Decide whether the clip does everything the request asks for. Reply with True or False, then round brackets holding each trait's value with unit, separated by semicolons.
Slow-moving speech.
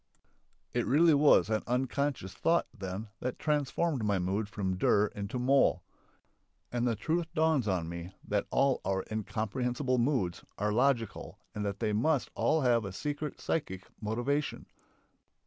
False (145 wpm)